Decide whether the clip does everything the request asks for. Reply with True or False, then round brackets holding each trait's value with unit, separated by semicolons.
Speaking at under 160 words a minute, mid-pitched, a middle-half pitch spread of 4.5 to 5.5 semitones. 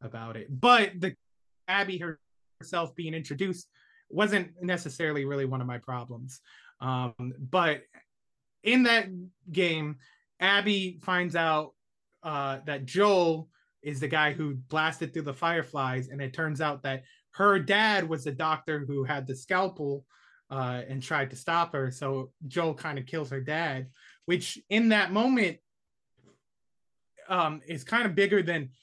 True (150 wpm; 155 Hz; 5.2 semitones)